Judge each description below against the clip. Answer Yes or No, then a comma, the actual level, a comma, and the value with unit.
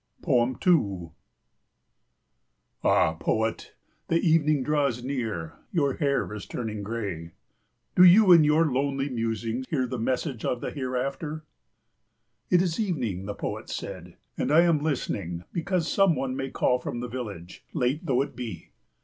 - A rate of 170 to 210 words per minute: No, average, 145 wpm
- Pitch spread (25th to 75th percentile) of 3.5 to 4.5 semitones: No, wide, 5.4 semitones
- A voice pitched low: Yes, low, 130 Hz